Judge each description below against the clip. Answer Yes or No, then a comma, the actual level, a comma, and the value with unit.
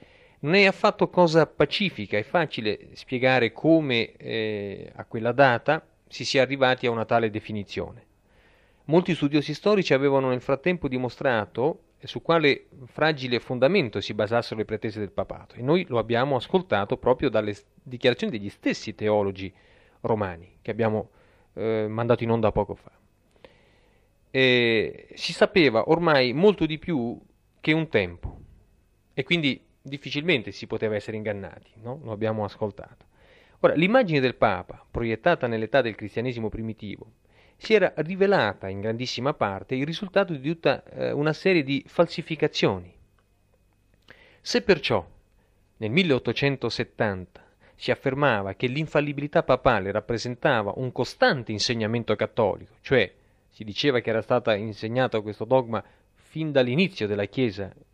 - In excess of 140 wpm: No, average, 135 wpm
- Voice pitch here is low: Yes, low, 120 Hz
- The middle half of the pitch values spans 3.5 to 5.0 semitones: No, wide, 5.6 semitones